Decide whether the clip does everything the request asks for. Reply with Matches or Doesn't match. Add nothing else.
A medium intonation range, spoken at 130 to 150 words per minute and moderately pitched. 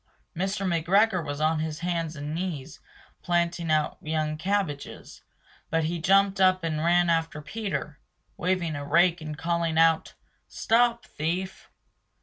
Matches